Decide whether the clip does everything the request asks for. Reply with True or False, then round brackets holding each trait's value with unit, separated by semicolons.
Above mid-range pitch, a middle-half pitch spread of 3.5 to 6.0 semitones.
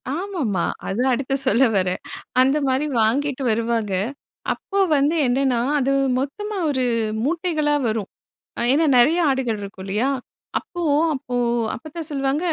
True (265 Hz; 4.3 semitones)